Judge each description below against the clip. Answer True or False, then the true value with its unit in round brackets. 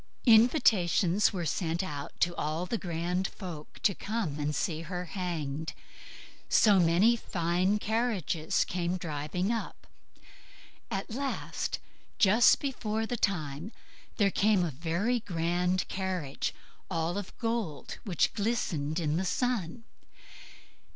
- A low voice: False (180 Hz)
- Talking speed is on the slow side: True (120 wpm)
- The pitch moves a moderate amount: True (4.5 semitones)